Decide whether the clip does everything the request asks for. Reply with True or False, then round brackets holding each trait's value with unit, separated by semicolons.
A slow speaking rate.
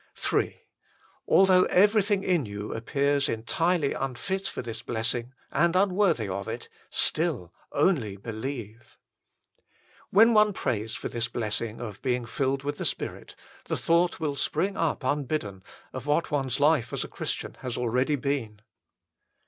False (150 wpm)